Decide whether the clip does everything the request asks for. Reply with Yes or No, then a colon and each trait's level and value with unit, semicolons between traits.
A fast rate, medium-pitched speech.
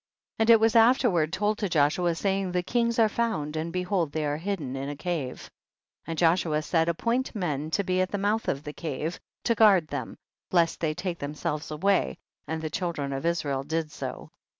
Yes: fast, 215 wpm; medium, 170 Hz